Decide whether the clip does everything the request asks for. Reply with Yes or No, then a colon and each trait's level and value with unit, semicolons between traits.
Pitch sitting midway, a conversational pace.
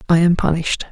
Yes: medium, 170 Hz; average, 195 wpm